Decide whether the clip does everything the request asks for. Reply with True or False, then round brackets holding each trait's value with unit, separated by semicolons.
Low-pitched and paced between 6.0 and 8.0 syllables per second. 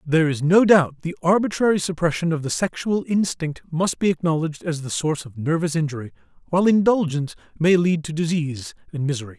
False (165 Hz; 6.1 syllables/s)